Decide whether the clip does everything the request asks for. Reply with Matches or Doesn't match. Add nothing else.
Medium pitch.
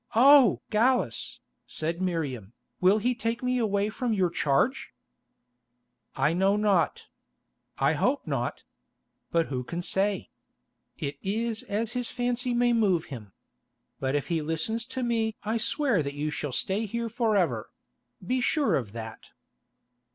Doesn't match